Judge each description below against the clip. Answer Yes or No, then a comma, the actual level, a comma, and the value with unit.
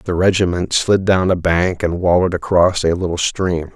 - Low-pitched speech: Yes, very low, 90 Hz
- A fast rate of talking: No, average, 190 wpm